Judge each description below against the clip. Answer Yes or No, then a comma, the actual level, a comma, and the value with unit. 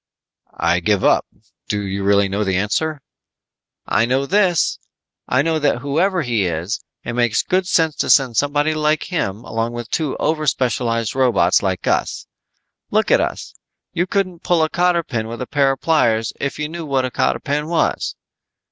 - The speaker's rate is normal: Yes, average, 180 wpm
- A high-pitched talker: No, low, 135 Hz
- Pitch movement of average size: No, wide, 6.0 semitones